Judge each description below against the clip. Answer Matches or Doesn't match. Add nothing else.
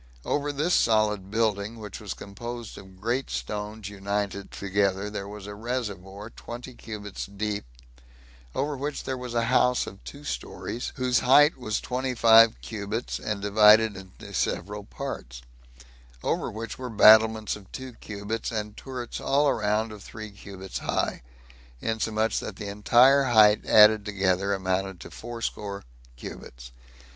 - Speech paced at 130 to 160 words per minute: Matches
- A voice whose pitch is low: Matches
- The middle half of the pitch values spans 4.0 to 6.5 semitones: Doesn't match